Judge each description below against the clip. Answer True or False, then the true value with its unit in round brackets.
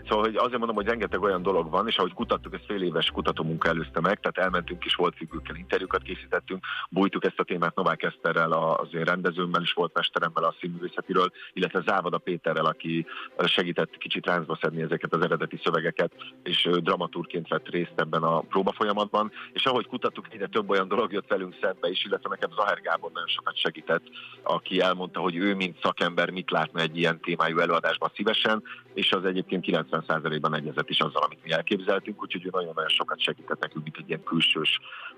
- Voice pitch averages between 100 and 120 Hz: False (90 Hz)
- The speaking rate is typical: False (190 wpm)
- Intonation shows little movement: False (4.5 semitones)